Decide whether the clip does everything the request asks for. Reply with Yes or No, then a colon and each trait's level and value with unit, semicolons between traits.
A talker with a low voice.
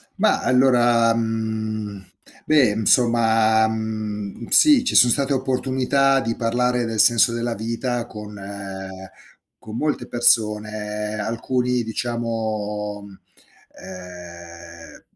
Yes: low, 115 Hz